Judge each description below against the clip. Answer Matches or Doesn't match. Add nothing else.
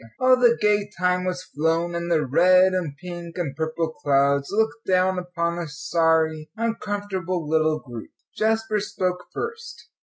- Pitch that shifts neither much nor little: Matches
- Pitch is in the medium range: Matches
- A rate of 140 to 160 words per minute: Matches